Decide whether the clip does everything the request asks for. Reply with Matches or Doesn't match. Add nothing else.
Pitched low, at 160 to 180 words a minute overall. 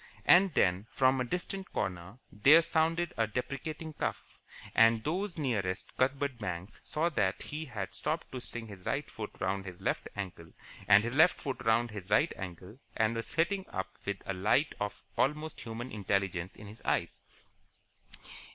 Matches